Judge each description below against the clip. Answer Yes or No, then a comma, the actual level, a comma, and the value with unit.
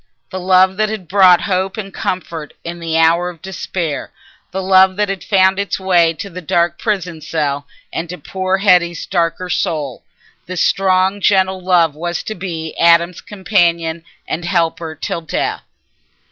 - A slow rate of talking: No, average, 160 wpm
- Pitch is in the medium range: Yes, medium, 180 Hz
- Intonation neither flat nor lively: No, narrow, 2.2 semitones